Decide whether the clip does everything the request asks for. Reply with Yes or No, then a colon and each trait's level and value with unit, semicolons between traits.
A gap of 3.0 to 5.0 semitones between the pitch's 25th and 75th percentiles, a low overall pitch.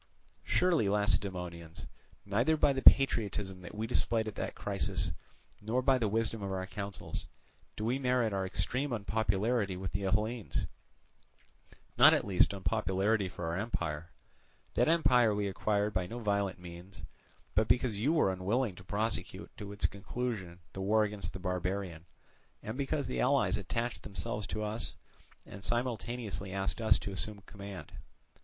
Yes: average, 3.3 semitones; low, 105 Hz